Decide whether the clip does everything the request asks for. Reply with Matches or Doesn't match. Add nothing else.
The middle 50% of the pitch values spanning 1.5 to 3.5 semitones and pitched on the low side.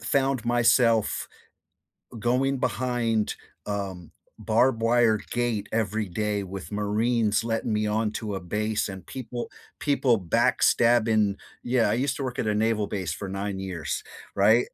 Matches